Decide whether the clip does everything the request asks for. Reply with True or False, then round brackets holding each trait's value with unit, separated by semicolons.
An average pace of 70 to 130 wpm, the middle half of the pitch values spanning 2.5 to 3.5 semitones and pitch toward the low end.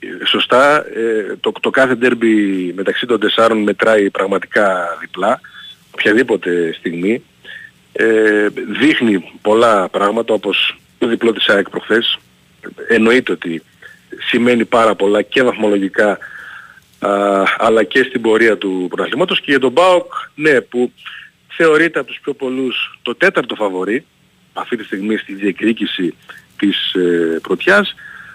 False (125 wpm; 4.9 semitones; 115 Hz)